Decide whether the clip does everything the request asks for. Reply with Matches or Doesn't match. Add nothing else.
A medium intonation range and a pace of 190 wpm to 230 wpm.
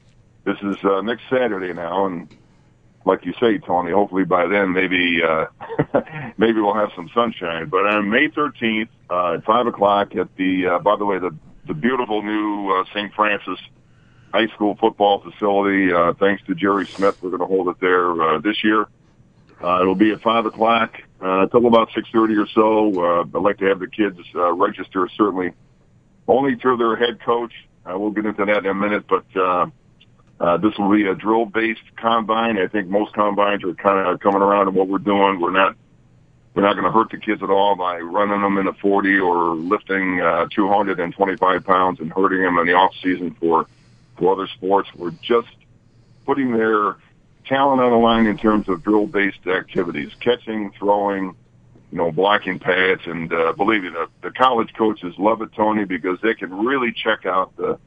Matches